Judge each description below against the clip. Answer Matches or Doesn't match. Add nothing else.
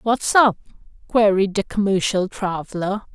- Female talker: Matches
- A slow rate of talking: Matches